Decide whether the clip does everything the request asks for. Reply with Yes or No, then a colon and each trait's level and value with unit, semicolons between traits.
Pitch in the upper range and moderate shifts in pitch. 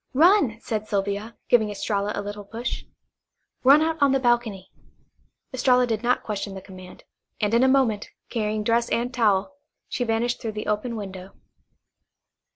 Yes: high, 225 Hz; average, 3.3 semitones